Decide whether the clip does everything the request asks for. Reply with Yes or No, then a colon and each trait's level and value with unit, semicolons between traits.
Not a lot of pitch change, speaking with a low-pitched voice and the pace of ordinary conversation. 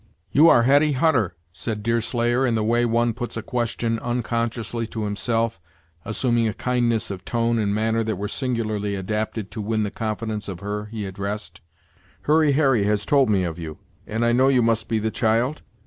Yes: narrow, 2.3 semitones; low, 115 Hz; average, 190 wpm